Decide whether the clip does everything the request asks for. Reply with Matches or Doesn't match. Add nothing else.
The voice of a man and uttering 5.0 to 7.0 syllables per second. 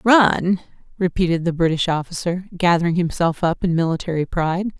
Doesn't match